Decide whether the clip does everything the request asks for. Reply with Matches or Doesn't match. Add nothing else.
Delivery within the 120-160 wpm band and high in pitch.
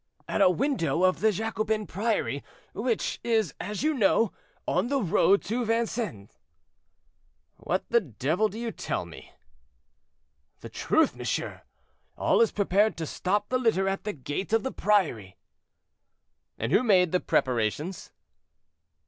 Matches